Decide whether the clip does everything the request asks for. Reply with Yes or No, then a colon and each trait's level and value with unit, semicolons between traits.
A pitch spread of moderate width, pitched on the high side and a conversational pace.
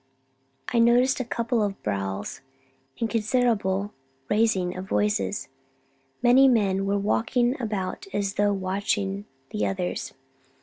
No: average, 3.7 semitones; high, 205 Hz; slow, 120 wpm